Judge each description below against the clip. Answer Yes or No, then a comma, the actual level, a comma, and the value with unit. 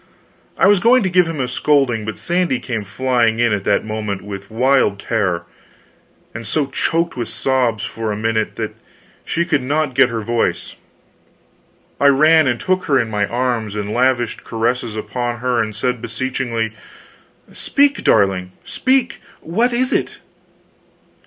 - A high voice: No, low, 125 Hz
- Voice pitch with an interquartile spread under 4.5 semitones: No, average, 5.2 semitones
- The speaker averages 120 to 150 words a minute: No, average, 160 wpm